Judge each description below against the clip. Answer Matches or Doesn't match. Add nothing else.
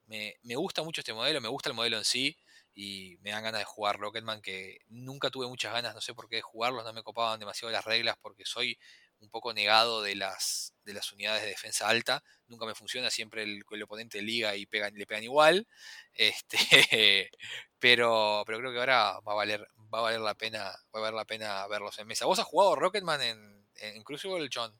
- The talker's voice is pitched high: Doesn't match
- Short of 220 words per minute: Doesn't match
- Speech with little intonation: Matches